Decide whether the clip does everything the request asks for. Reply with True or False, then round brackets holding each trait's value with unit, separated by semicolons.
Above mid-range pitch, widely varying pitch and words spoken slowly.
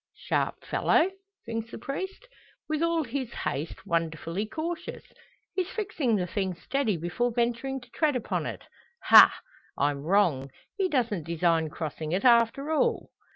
False (230 Hz; 8.7 semitones; 145 wpm)